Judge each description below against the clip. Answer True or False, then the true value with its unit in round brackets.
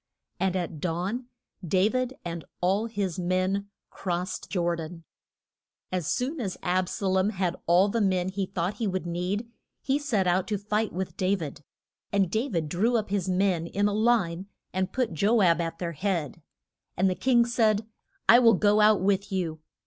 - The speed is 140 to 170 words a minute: False (185 wpm)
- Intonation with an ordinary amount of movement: True (3.1 semitones)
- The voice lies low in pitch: False (190 Hz)